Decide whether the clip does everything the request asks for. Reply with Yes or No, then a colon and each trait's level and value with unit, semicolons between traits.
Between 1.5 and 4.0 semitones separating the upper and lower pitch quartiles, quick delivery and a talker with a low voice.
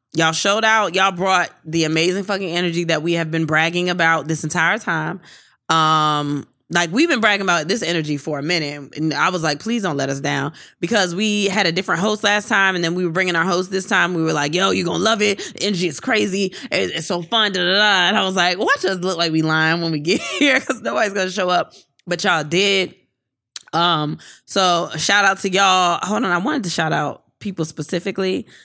No: average, 3.4 semitones; fast, 235 wpm; medium, 175 Hz